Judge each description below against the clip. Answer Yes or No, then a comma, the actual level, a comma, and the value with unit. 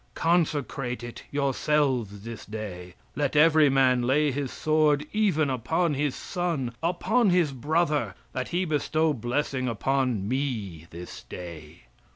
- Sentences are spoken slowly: Yes, slow, 130 wpm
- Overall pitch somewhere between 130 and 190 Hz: Yes, low, 135 Hz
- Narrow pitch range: No, average, 4.4 semitones